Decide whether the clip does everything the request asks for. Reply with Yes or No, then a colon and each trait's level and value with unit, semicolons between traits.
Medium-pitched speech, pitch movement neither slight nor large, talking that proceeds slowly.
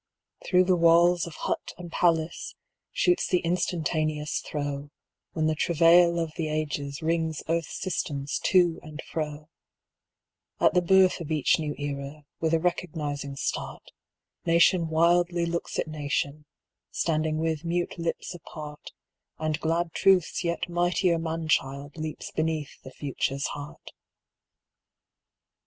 No: medium, 160 Hz; narrow, 2.3 semitones; slow, 130 wpm